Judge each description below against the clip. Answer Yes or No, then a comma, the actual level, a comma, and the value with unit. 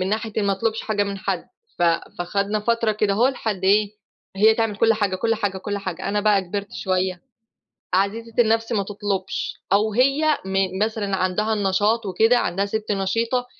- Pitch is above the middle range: Yes, high, 205 Hz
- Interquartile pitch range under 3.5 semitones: Yes, narrow, 2.4 semitones